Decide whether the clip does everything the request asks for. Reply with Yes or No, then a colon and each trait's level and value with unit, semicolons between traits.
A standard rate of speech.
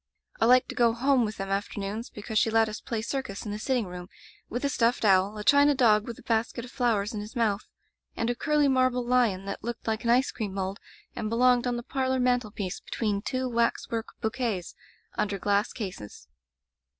No: fast, 210 wpm